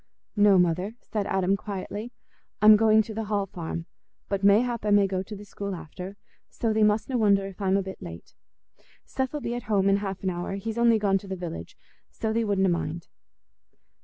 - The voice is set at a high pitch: Yes, high, 200 Hz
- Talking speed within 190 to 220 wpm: Yes, average, 200 wpm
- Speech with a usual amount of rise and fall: No, narrow, 2.3 semitones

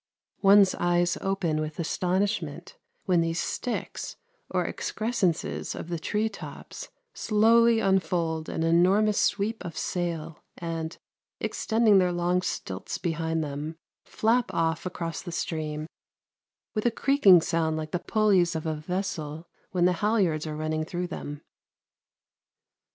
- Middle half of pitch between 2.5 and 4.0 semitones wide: Yes, average, 3.6 semitones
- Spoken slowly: Yes, slow, 130 wpm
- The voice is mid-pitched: Yes, medium, 175 Hz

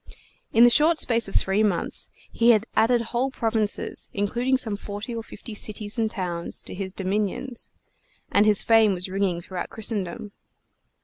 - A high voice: Yes, high, 215 Hz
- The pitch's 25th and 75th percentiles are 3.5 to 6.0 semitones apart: No, average, 2.9 semitones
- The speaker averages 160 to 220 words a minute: Yes, average, 165 wpm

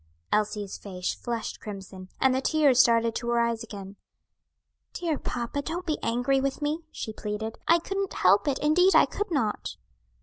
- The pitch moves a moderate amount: No, wide, 5.9 semitones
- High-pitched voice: Yes, high, 240 Hz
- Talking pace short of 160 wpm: No, average, 170 wpm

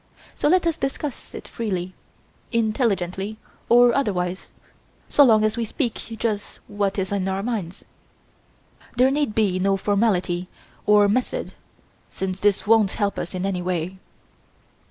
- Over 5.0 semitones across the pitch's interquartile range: No, average, 3.6 semitones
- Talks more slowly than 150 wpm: Yes, average, 140 wpm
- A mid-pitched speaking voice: No, high, 205 Hz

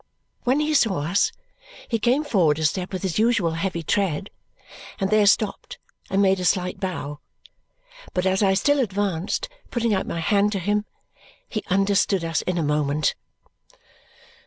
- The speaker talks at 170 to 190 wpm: No, average, 160 wpm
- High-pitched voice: Yes, high, 195 Hz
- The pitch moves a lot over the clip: No, average, 3.6 semitones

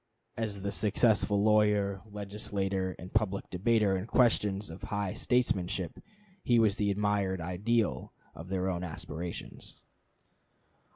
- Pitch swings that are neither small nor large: No, narrow, 2.2 semitones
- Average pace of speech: No, slow, 120 wpm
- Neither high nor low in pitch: No, low, 100 Hz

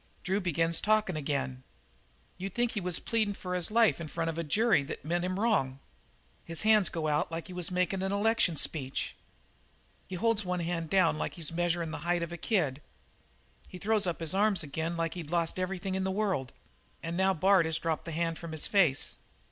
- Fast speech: Yes, fast, 210 wpm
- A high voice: No, medium, 175 Hz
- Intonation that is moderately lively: Yes, average, 3.0 semitones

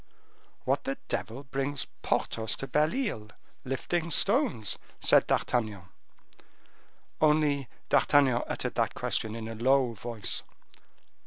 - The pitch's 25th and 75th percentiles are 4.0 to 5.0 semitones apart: Yes, average, 4.7 semitones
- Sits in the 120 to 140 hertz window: Yes, low, 135 Hz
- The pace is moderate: No, slow, 110 wpm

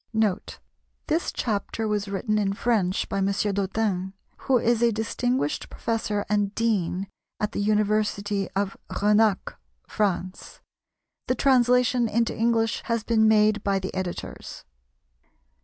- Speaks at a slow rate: Yes, slow, 125 wpm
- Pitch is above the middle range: Yes, high, 210 Hz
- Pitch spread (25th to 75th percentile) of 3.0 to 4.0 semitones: No, narrow, 2.4 semitones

